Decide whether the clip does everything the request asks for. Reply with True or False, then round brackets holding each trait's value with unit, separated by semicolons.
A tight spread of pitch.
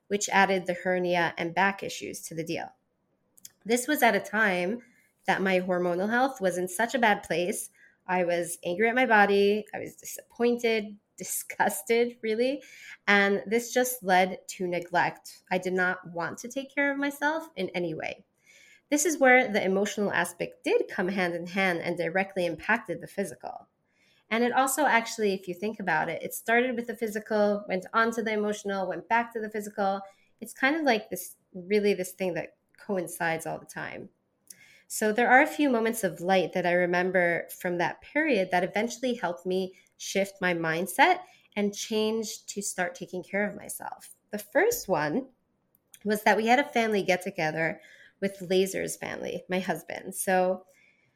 False (4.1 semitones)